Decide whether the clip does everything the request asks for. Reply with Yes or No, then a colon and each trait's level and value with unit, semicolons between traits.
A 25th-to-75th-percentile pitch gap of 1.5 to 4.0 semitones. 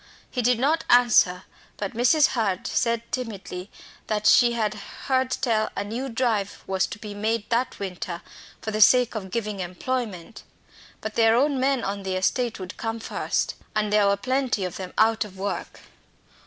Yes: average, 3.5 semitones